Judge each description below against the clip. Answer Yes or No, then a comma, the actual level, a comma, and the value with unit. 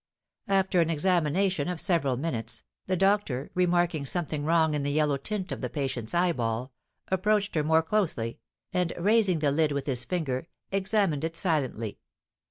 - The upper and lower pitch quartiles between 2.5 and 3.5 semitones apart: No, average, 4.6 semitones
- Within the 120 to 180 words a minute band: Yes, average, 160 wpm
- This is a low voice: No, medium, 160 Hz